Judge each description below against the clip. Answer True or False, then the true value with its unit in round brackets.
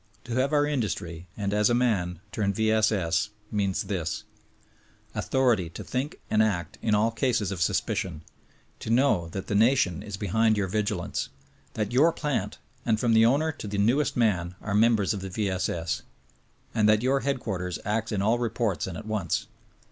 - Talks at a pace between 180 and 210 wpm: True (190 wpm)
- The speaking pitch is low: True (105 Hz)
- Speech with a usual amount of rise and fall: True (3.7 semitones)